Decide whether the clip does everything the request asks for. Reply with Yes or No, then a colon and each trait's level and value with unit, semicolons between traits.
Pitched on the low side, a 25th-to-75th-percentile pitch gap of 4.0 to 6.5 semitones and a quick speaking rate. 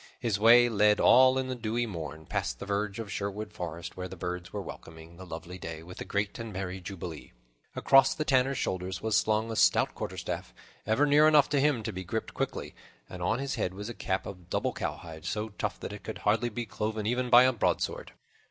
Yes: low, 105 Hz; average, 4.8 semitones; fast, 220 wpm